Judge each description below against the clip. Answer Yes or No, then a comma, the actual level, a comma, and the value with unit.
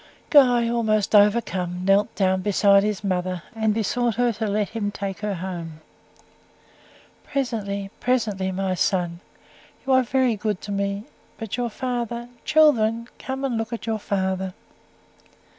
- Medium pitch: No, high, 210 Hz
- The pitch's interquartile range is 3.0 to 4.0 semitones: Yes, average, 3.5 semitones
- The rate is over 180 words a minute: No, average, 145 wpm